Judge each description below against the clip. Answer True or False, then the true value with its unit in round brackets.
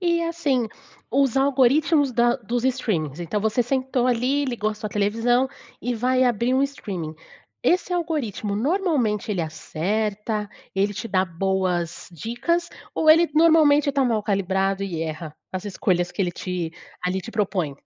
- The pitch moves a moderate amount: False (5.9 semitones)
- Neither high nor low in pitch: False (225 Hz)